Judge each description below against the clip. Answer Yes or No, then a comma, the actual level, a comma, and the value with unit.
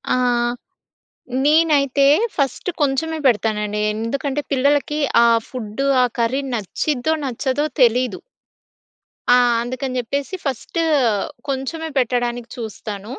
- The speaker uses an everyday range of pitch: Yes, average, 3.2 semitones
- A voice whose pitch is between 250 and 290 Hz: Yes, very high, 255 Hz